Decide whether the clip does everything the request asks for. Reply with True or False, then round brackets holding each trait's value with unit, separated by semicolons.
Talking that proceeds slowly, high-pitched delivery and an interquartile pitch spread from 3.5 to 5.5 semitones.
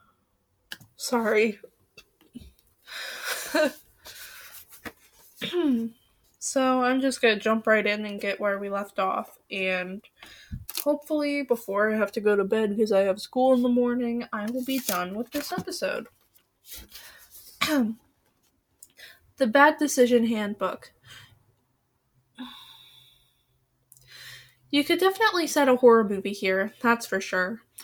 True (115 wpm; 225 Hz; 5.2 semitones)